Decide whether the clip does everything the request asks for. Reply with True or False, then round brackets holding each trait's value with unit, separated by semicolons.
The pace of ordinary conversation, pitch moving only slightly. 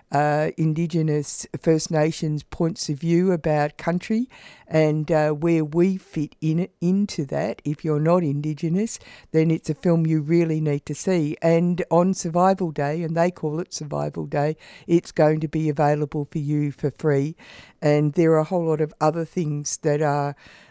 True (175 wpm; 2.2 semitones)